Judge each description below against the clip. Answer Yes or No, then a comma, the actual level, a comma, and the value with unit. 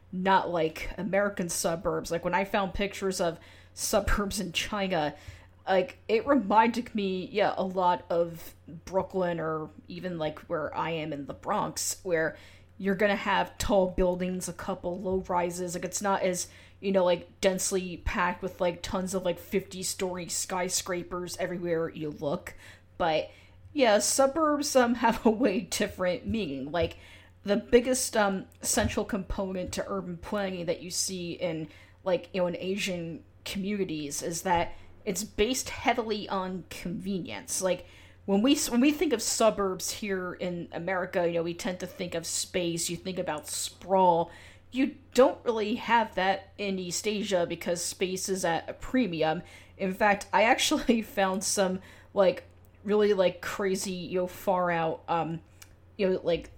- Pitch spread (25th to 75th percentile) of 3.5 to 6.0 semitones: No, average, 2.9 semitones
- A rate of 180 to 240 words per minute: No, average, 160 wpm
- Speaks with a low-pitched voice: No, medium, 185 Hz